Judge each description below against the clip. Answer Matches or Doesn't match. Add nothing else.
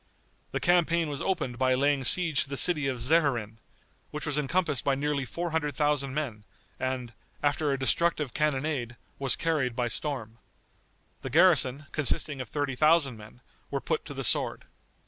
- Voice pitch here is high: Doesn't match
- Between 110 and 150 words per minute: Doesn't match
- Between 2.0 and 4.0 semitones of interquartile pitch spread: Matches